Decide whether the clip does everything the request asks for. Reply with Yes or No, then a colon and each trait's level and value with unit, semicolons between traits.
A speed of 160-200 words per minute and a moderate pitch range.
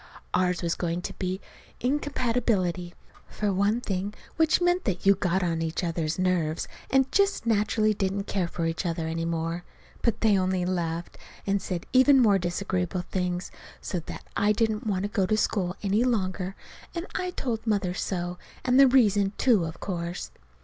Yes: average, 175 wpm; average, 3.8 semitones